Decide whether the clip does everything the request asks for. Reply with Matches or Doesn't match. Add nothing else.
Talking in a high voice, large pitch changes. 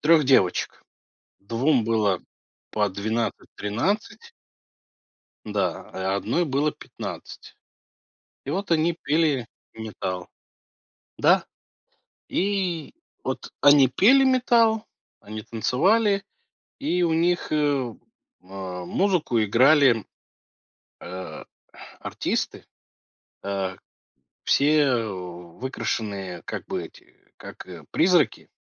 Doesn't match